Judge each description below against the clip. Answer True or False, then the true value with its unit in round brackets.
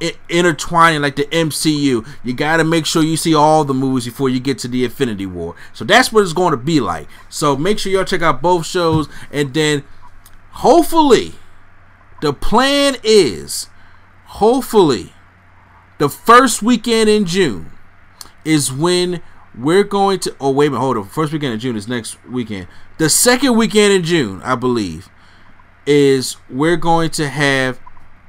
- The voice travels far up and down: True (6.8 semitones)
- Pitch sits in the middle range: True (150 Hz)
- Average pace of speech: True (165 wpm)